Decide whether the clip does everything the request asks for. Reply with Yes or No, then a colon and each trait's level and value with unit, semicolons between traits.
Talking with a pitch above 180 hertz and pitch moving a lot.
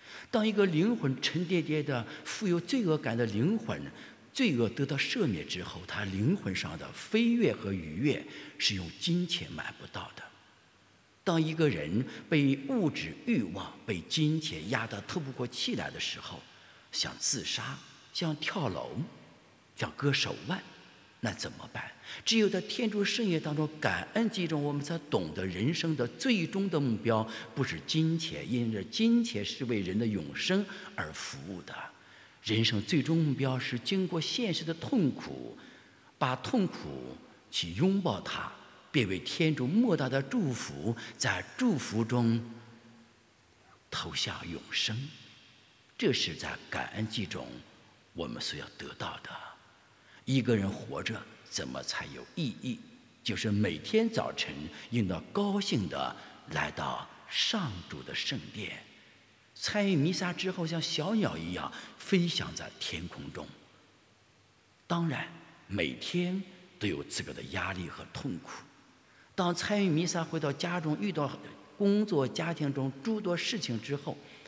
No: medium, 150 Hz; wide, 7.9 semitones